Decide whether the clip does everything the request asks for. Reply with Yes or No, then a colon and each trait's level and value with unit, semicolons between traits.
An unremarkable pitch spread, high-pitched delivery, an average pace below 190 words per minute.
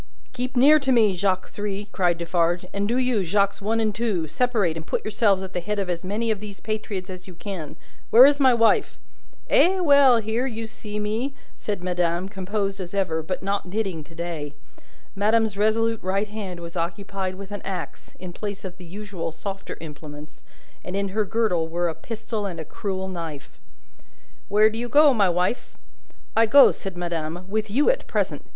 No: average, 3.7 semitones; high, 200 Hz; average, 195 wpm